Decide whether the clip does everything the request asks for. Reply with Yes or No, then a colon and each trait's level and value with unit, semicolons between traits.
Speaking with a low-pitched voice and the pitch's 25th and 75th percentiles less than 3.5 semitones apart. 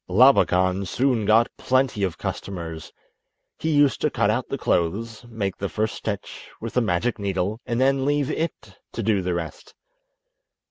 No: low, 110 Hz; average, 5.2 semitones